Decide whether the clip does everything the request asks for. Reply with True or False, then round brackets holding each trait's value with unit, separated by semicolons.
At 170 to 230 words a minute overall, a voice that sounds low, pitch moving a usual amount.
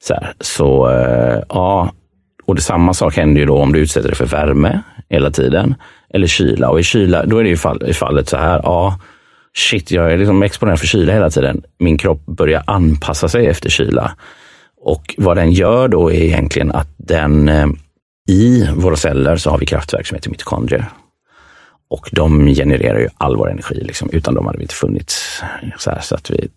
True (200 wpm; 80 Hz; 3.5 semitones)